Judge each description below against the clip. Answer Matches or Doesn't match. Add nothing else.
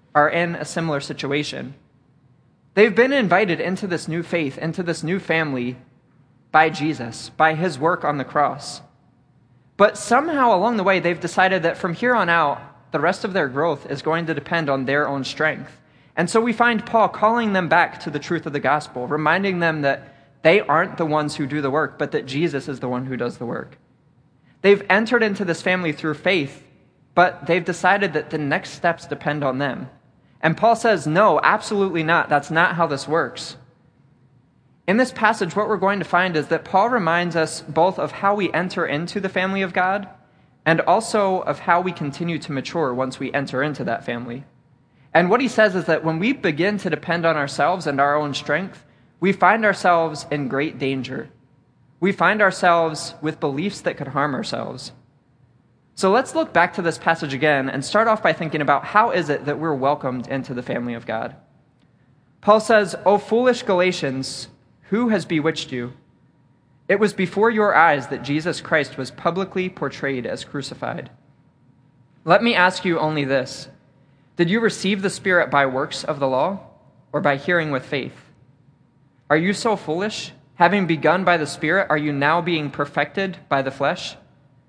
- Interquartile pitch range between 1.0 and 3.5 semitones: Doesn't match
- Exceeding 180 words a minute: Matches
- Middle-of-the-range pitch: Matches